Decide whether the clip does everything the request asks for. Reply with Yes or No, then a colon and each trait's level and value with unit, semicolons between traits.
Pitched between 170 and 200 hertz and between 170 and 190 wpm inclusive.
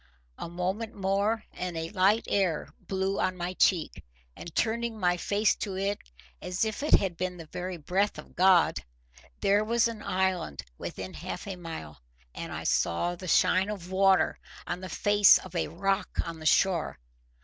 Yes: medium, 185 Hz; average, 175 wpm